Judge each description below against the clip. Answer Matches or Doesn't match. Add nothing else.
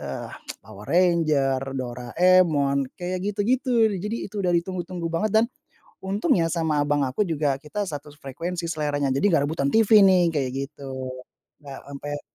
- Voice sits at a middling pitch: Matches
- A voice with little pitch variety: Doesn't match